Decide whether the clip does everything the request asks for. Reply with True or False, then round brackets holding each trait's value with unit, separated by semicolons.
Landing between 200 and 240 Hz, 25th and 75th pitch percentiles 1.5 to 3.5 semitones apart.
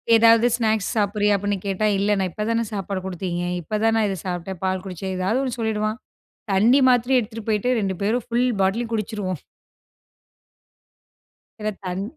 True (210 Hz; 3.0 semitones)